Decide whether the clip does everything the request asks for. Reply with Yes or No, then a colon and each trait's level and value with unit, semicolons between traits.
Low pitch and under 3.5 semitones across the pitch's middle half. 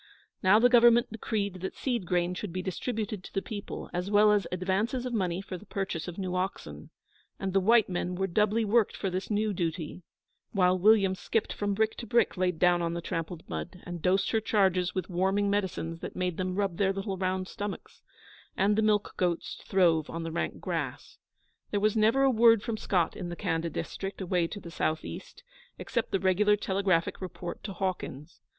No: high, 190 Hz; average, 2.8 semitones